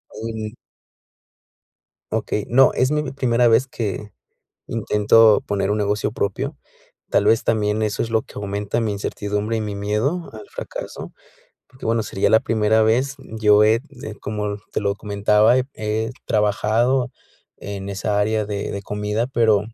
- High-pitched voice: No, low, 110 Hz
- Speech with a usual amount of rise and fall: No, narrow, 1.9 semitones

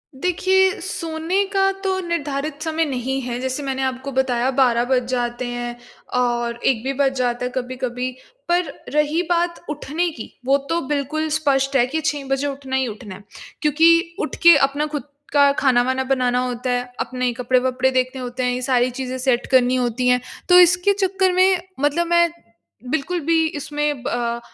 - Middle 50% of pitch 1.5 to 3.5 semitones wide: No, average, 4.1 semitones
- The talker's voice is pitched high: Yes, very high, 270 Hz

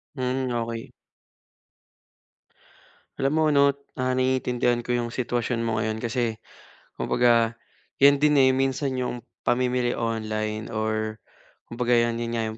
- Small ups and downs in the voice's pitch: Yes, narrow, 2.1 semitones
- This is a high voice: No, low, 120 Hz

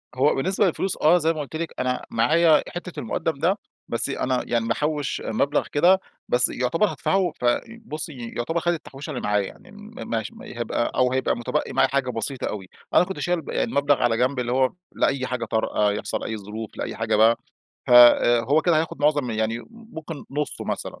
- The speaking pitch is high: No, low, 135 Hz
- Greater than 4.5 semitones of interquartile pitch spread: Yes, wide, 5.4 semitones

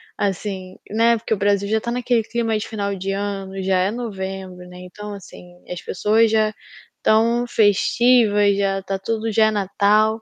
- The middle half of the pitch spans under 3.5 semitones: Yes, narrow, 2.4 semitones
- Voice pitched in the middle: No, high, 210 Hz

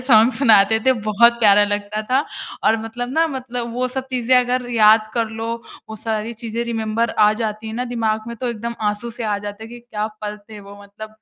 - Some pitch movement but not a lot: No, narrow, 2.1 semitones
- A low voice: No, high, 225 Hz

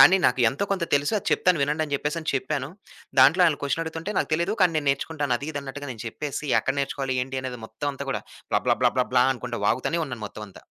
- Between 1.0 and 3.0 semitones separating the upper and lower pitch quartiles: No, average, 3.4 semitones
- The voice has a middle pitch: Yes, medium, 145 Hz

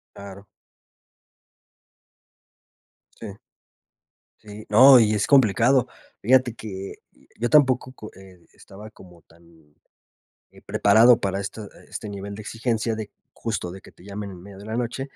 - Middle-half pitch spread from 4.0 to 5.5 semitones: No, average, 3.2 semitones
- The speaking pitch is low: Yes, low, 105 Hz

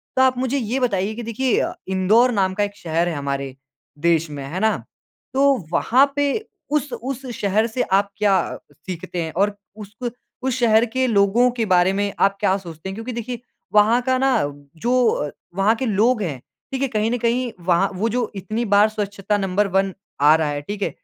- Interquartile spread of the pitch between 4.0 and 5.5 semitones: Yes, average, 4.3 semitones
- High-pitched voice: Yes, high, 210 Hz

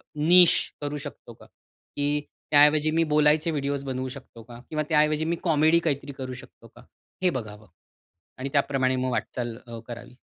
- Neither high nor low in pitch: Yes, medium, 145 Hz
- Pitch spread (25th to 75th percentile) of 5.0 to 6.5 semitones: No, average, 3.0 semitones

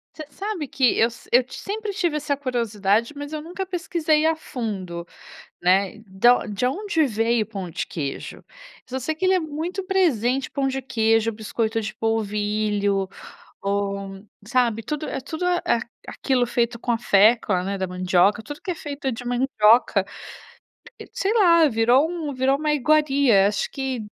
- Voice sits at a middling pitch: No, high, 245 Hz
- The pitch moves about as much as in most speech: No, wide, 6.3 semitones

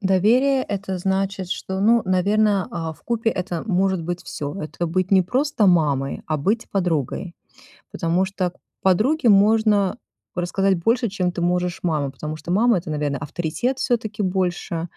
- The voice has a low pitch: No, high, 190 Hz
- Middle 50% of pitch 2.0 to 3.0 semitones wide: No, average, 3.4 semitones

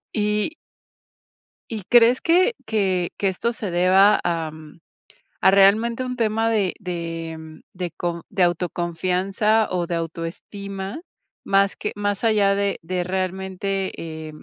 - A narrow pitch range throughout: No, average, 3.3 semitones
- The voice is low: No, high, 190 Hz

